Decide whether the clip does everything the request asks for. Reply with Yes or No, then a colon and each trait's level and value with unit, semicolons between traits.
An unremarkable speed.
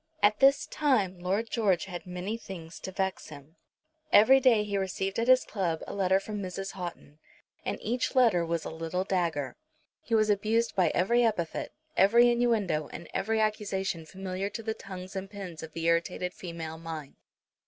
Yes: average, 175 wpm